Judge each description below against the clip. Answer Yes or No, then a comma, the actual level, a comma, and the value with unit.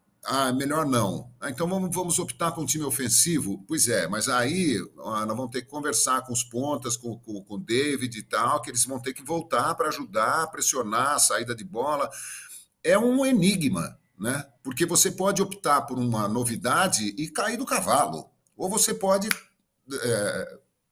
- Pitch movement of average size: No, wide, 7.0 semitones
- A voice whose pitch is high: No, medium, 145 Hz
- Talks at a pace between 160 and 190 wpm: Yes, average, 180 wpm